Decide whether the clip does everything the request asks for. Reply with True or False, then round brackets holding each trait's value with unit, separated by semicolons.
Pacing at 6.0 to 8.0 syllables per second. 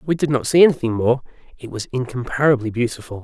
True (6.4 syllables/s)